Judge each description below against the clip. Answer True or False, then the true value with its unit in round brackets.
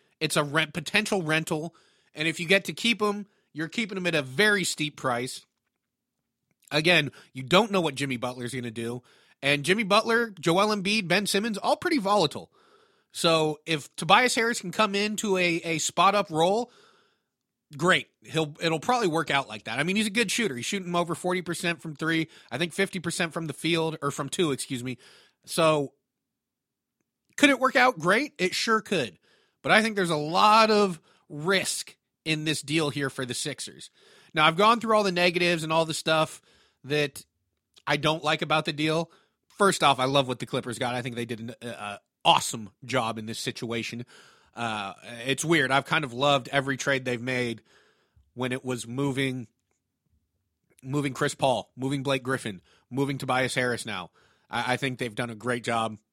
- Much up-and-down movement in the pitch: True (6.4 semitones)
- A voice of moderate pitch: True (155 Hz)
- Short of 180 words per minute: False (190 wpm)